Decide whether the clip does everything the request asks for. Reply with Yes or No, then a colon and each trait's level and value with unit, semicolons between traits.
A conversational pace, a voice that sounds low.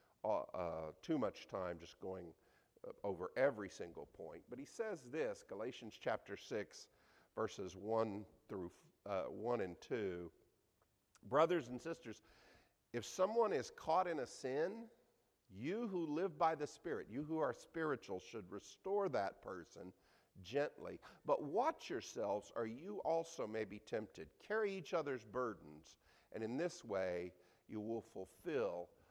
Yes: average, 145 wpm; low, 125 Hz